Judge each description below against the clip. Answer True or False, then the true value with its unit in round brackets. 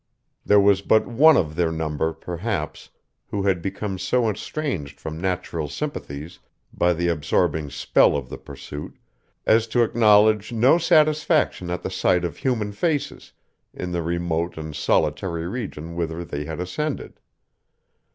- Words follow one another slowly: False (145 wpm)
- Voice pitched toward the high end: False (90 Hz)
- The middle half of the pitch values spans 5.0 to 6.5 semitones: True (5.5 semitones)